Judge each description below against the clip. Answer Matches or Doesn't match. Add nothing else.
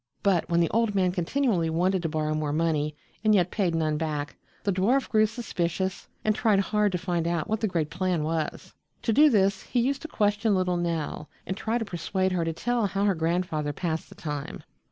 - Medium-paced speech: Doesn't match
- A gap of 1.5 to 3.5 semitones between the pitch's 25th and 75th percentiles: Doesn't match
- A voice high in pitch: Doesn't match